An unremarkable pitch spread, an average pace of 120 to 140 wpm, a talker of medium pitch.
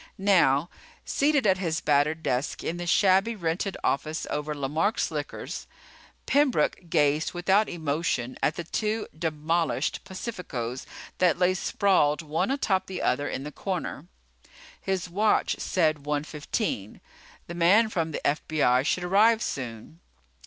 Yes: average, 4.4 semitones; slow, 135 wpm; medium, 170 Hz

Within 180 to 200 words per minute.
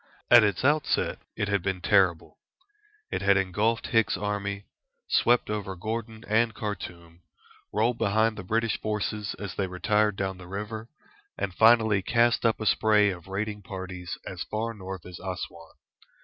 No: average, 155 wpm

